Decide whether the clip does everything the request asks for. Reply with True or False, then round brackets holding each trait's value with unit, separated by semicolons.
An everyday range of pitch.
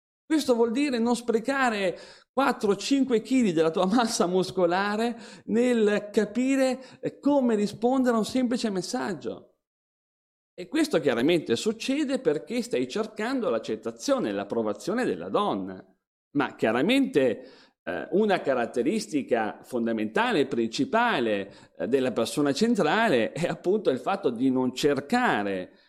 False (6.3 semitones)